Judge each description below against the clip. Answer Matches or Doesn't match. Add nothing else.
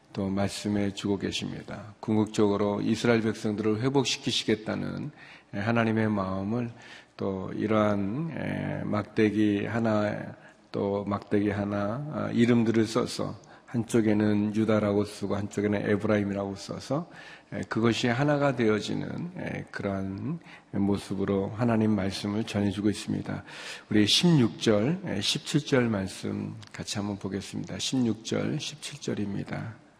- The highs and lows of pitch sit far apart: Doesn't match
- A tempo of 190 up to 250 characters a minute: Doesn't match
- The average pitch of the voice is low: Matches